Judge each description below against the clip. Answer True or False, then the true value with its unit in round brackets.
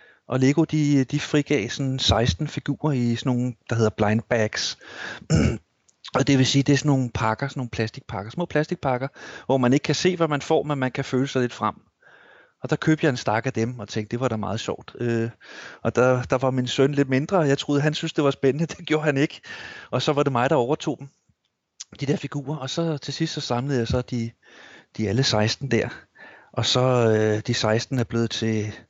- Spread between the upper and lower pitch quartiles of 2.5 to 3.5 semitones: False (3.9 semitones)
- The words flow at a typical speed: False (235 wpm)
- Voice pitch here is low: True (130 Hz)